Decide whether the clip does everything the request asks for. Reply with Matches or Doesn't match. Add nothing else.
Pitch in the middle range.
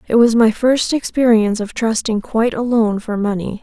Doesn't match